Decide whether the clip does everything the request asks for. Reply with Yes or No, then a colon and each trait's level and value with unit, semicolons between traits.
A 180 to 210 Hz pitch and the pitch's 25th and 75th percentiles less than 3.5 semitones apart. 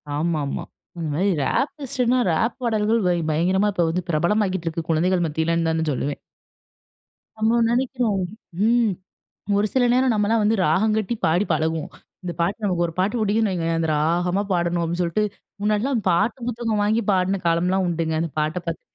No: medium, 185 Hz; average, 4.7 semitones